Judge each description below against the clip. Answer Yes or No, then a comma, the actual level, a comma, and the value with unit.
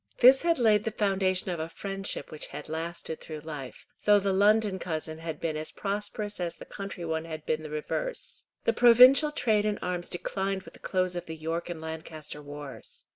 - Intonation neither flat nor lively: Yes, average, 4.6 semitones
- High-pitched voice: No, medium, 180 Hz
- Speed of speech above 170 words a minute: Yes, average, 200 wpm